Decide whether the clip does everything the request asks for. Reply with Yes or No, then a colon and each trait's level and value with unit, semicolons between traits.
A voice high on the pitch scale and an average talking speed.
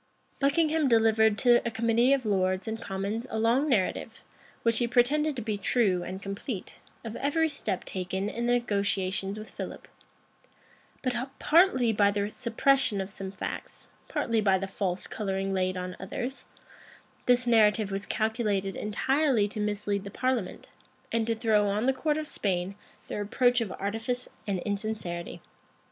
Yes: high, 220 Hz; average, 155 wpm